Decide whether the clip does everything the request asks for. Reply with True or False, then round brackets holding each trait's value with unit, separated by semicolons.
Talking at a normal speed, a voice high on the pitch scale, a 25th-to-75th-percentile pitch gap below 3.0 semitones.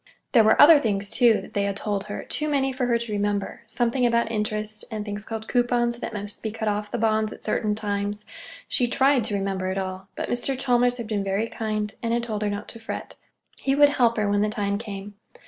False (230 wpm; 215 Hz; 2.6 semitones)